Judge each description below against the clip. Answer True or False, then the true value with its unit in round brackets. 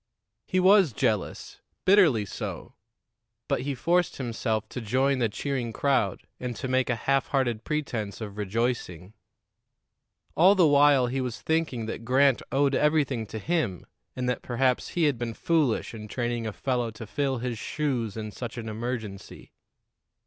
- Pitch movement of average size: True (4.0 semitones)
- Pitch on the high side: False (125 Hz)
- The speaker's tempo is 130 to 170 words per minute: True (160 wpm)